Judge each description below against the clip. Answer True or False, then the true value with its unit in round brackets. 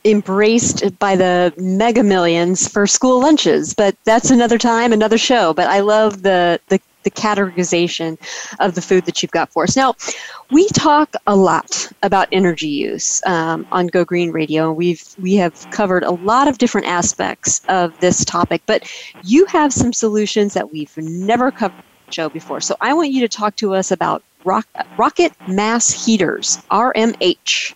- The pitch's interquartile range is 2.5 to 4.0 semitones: False (4.5 semitones)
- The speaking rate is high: False (170 wpm)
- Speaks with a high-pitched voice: True (200 Hz)